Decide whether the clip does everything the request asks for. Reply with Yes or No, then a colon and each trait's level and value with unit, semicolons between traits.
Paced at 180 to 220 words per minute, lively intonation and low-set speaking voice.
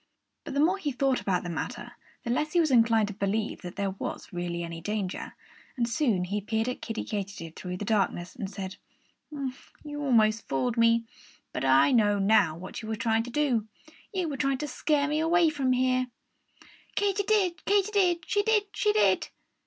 No: average, 195 wpm; wide, 6.9 semitones; high, 235 Hz